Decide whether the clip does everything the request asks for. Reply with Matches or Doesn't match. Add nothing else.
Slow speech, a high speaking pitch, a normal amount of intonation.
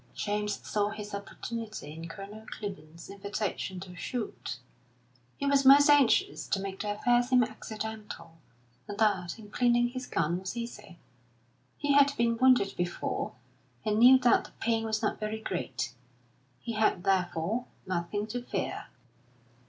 Doesn't match